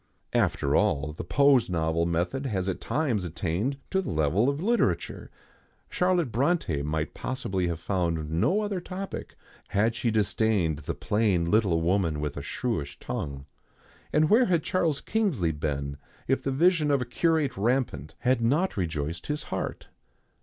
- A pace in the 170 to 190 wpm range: No, average, 155 wpm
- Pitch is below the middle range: Yes, low, 105 Hz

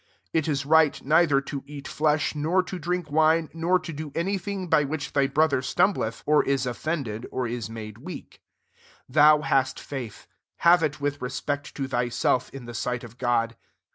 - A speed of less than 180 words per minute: No, average, 190 wpm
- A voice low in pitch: No, medium, 145 Hz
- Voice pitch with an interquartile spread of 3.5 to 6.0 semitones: Yes, average, 3.9 semitones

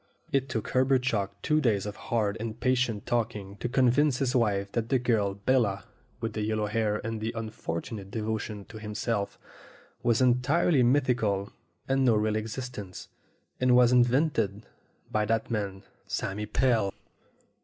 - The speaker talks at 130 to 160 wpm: Yes, average, 155 wpm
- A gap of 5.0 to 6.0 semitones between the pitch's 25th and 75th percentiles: No, average, 3.2 semitones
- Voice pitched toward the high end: No, low, 115 Hz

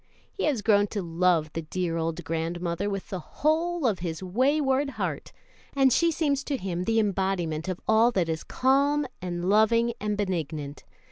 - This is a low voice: No, high, 195 Hz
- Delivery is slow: No, average, 175 wpm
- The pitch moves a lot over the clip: Yes, wide, 7.3 semitones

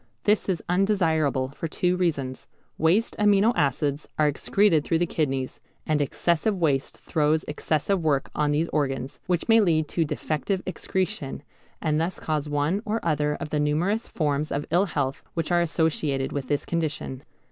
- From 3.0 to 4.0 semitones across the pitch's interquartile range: Yes, average, 3.5 semitones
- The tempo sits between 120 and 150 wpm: No, average, 165 wpm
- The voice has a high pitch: No, medium, 155 Hz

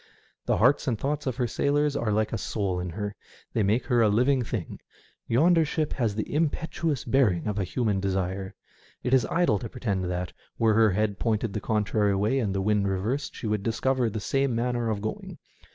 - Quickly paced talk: Yes, fast, 210 wpm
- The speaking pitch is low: Yes, low, 110 Hz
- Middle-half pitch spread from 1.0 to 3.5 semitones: No, average, 4.3 semitones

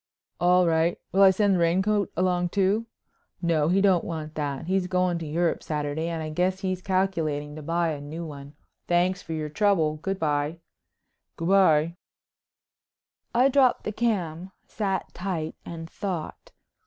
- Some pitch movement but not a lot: Yes, average, 3.3 semitones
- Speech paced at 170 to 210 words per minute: No, average, 160 wpm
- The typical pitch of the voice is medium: Yes, medium, 175 Hz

